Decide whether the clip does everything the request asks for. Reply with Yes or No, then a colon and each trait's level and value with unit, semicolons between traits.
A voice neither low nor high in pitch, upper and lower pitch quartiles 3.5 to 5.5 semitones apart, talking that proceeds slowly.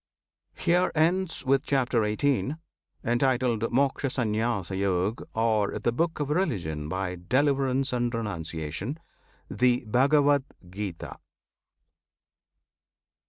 No: low, 120 Hz; average, 5.1 semitones; slow, 85 wpm